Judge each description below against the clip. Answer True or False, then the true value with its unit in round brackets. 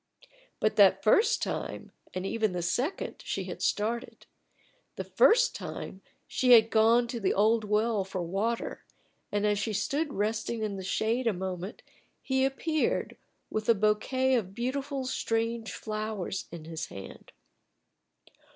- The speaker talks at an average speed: True (145 wpm)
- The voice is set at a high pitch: True (220 Hz)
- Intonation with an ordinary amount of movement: True (3.5 semitones)